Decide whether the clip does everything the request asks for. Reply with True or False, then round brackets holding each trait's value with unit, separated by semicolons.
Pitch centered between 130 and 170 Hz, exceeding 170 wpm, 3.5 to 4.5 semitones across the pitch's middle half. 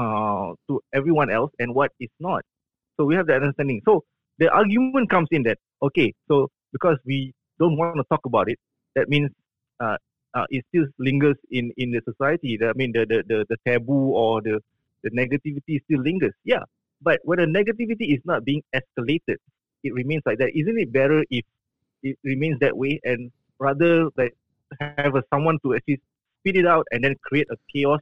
True (140 Hz; 195 wpm; 3.8 semitones)